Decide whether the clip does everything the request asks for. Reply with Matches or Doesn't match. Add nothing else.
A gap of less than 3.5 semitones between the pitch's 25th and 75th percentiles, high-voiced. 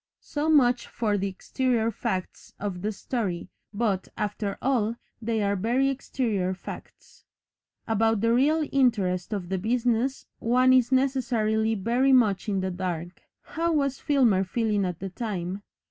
Doesn't match